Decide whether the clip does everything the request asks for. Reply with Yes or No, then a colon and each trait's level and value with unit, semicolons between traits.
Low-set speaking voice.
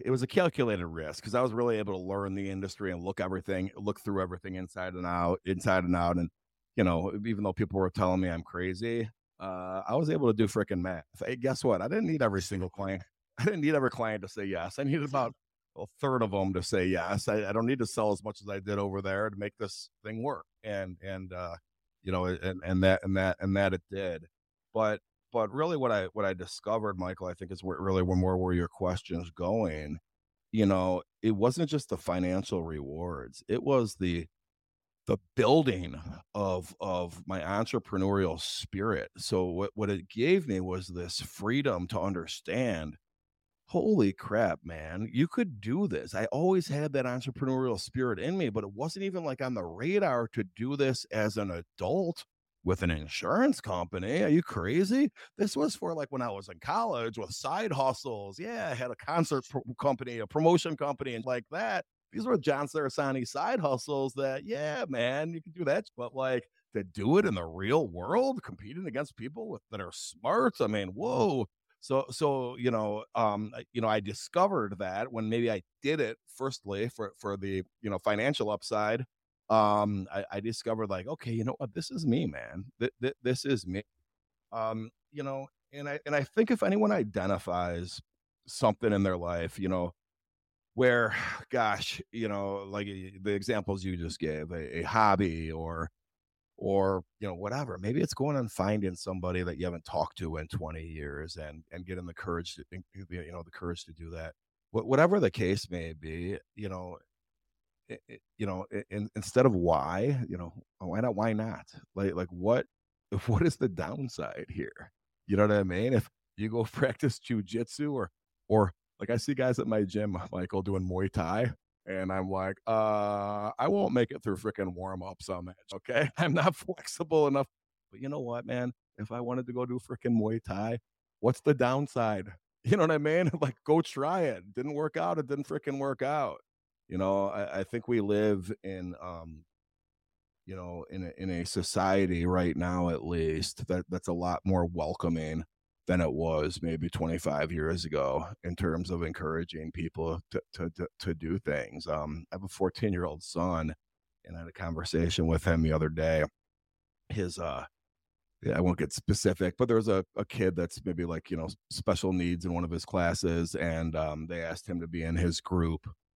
Yes: very low, 95 Hz